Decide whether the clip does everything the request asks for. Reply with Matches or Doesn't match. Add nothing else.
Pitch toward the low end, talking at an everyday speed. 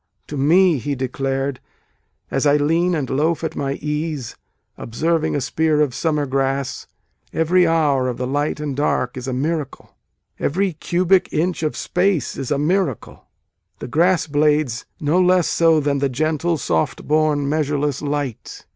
Doesn't match